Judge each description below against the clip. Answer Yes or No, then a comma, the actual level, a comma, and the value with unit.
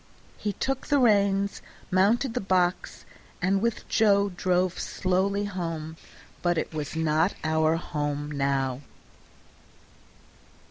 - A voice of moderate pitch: Yes, medium, 180 Hz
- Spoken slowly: Yes, slow, 110 wpm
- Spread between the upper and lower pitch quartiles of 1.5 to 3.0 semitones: No, average, 4.2 semitones